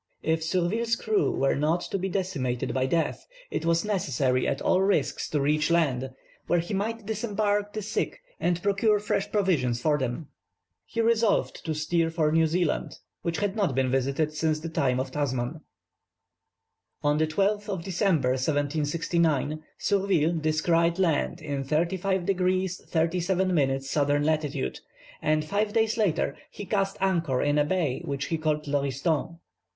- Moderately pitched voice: Yes, medium, 165 Hz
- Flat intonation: No, average, 4.7 semitones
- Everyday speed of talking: Yes, average, 155 wpm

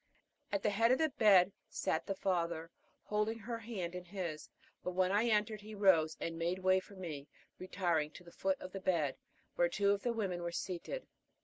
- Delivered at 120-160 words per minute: No, fast, 205 wpm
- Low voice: No, medium, 185 Hz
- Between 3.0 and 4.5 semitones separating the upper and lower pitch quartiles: Yes, average, 3.4 semitones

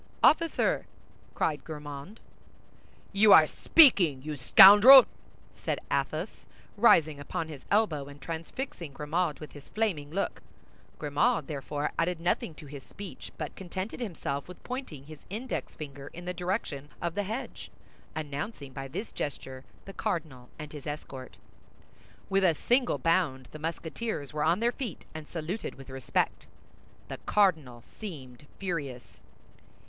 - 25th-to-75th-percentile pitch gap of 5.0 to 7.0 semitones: Yes, wide, 5.4 semitones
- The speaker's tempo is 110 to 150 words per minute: Yes, average, 140 wpm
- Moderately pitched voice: Yes, medium, 160 Hz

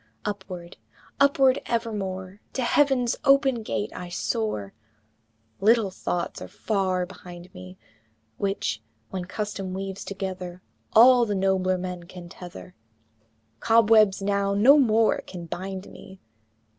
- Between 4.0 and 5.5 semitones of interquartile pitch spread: No, average, 3.6 semitones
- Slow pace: Yes, slow, 120 wpm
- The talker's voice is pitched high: Yes, high, 195 Hz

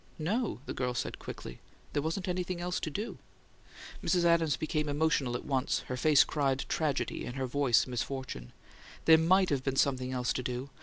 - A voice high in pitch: No, medium, 145 Hz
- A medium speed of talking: Yes, average, 185 wpm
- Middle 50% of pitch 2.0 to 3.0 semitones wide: No, average, 4.2 semitones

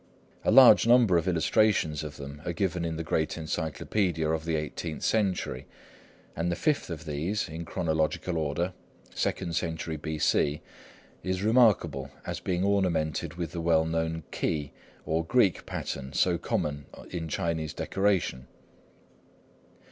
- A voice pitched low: Yes, very low, 80 Hz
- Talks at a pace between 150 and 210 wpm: No, average, 140 wpm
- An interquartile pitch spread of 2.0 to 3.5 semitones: Yes, average, 2.9 semitones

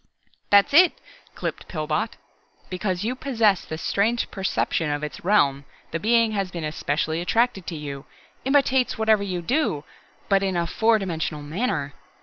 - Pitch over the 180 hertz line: Yes, high, 190 Hz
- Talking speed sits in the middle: Yes, average, 150 wpm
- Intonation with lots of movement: Yes, wide, 6.0 semitones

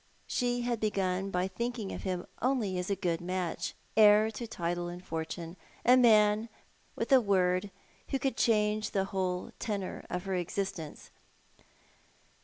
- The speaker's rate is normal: Yes, average, 150 wpm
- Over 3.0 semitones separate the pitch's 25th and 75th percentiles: Yes, average, 3.4 semitones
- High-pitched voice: Yes, high, 195 Hz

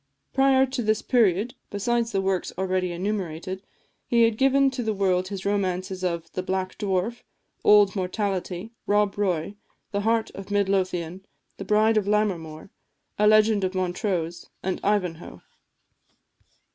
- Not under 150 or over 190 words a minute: No, average, 140 wpm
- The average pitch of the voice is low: No, high, 195 Hz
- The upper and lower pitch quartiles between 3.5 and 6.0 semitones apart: No, average, 2.7 semitones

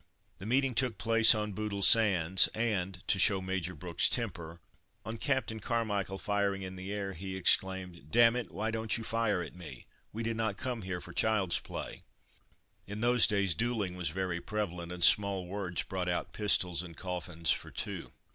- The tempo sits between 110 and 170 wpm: No, average, 180 wpm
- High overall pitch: No, very low, 95 Hz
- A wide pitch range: No, average, 3.6 semitones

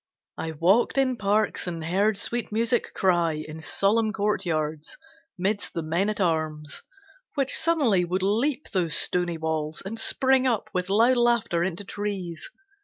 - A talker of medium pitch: No, high, 195 Hz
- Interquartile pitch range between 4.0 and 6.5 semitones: Yes, average, 5.2 semitones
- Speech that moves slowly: No, average, 150 wpm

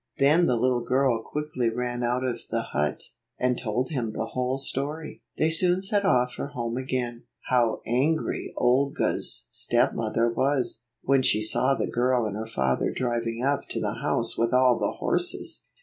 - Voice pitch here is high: No, low, 125 Hz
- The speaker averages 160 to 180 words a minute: Yes, average, 170 wpm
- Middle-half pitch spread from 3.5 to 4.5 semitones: No, average, 2.7 semitones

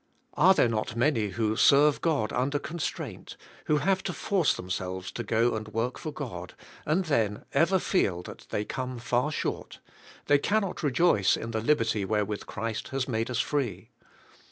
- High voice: No, low, 120 Hz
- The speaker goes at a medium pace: Yes, average, 180 wpm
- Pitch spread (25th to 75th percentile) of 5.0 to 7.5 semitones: Yes, wide, 5.6 semitones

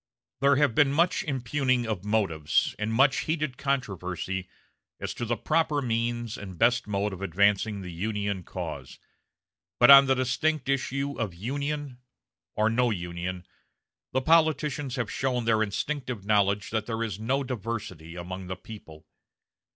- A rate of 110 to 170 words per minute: Yes, average, 150 wpm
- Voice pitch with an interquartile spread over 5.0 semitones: Yes, wide, 5.4 semitones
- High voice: No, low, 115 Hz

